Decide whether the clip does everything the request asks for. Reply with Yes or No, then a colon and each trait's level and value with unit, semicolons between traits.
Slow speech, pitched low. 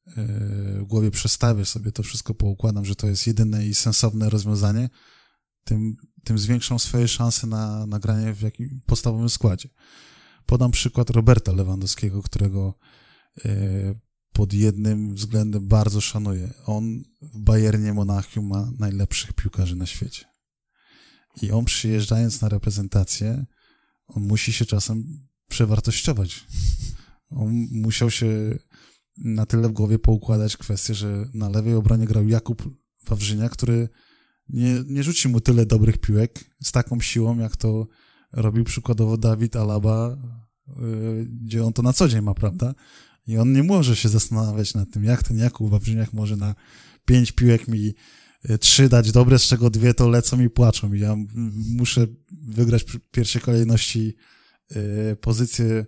No: average, 140 wpm; low, 110 Hz